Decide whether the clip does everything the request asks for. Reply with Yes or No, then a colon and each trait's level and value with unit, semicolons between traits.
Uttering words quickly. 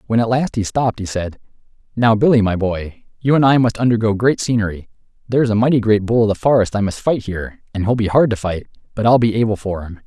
Yes: fast, 250 wpm